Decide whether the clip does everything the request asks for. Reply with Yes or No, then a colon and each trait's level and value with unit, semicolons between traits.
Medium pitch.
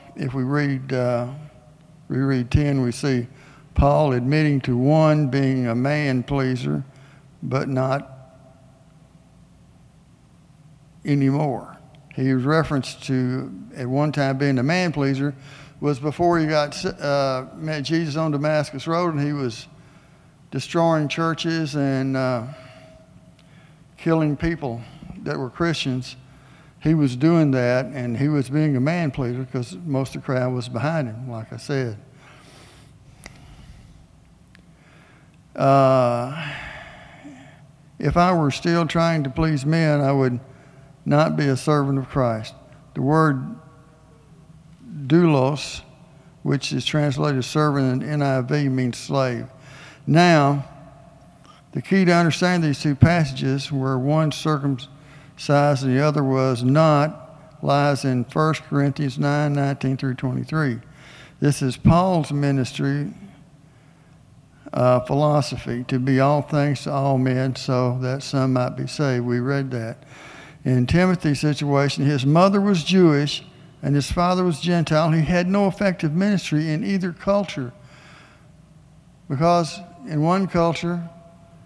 Yes: medium, 145 Hz